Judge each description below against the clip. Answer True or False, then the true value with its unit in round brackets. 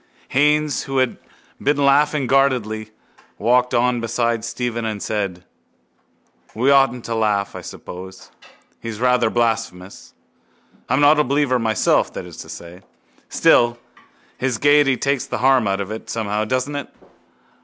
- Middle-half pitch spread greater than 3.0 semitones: True (3.9 semitones)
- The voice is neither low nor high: False (120 Hz)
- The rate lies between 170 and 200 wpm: False (145 wpm)